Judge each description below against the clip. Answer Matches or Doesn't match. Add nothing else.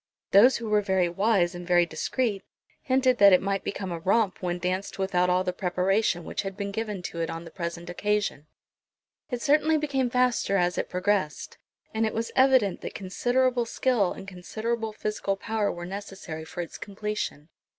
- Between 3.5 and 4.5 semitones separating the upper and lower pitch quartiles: Matches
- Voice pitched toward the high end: Matches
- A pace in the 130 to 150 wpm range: Doesn't match